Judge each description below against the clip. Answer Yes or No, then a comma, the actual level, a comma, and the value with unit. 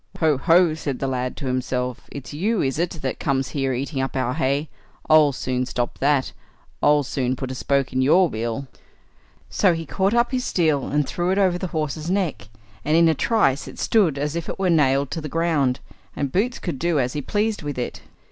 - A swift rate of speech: Yes, fast, 215 wpm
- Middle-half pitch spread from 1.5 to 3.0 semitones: No, average, 4.4 semitones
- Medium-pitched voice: Yes, medium, 145 Hz